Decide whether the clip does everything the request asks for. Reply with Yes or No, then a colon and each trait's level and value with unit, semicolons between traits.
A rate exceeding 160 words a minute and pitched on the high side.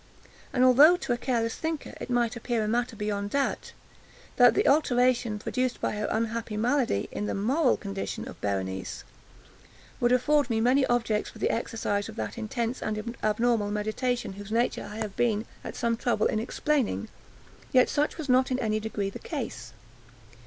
Yes: average, 175 wpm; high, 230 Hz